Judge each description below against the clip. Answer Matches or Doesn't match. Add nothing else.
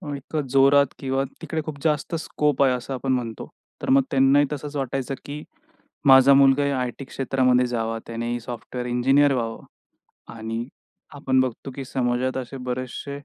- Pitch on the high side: Doesn't match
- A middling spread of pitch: Doesn't match